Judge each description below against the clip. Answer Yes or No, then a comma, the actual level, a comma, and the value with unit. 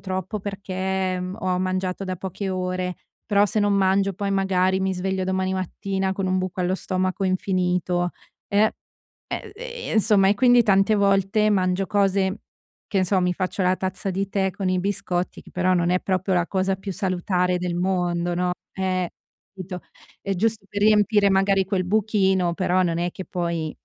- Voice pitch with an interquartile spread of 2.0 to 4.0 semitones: No, narrow, 1.3 semitones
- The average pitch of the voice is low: No, high, 190 Hz